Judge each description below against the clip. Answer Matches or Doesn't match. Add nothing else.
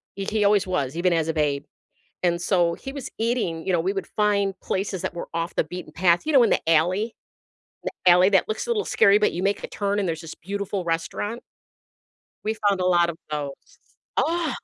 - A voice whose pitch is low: Doesn't match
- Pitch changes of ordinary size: Matches